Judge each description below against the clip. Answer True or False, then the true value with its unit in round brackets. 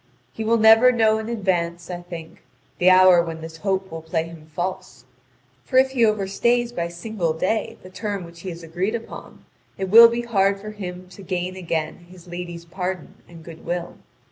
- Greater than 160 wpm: True (190 wpm)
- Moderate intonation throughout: True (4.0 semitones)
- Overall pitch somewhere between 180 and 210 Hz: True (185 Hz)